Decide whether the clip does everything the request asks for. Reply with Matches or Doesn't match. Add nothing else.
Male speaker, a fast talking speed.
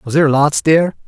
Matches